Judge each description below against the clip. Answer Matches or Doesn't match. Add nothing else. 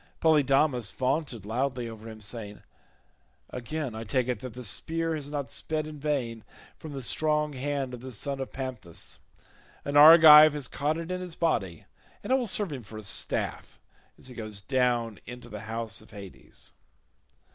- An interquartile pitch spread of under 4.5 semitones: Doesn't match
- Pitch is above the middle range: Doesn't match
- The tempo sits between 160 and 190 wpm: Matches